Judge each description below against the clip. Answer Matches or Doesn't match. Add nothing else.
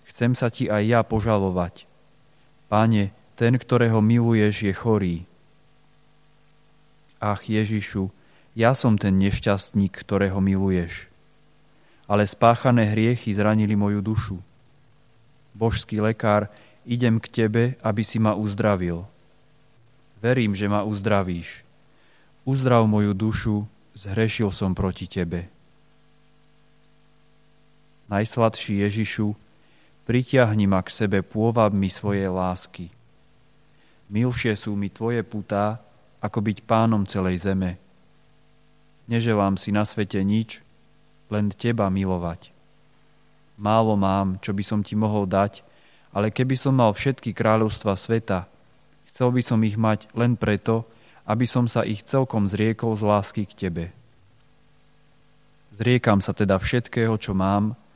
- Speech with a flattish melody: Doesn't match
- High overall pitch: Doesn't match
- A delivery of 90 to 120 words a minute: Matches